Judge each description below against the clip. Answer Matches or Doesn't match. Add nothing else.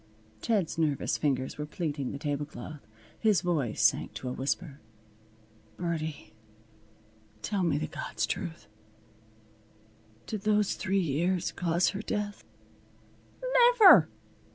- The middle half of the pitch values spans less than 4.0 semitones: Doesn't match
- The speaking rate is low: Matches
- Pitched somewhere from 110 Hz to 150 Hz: Doesn't match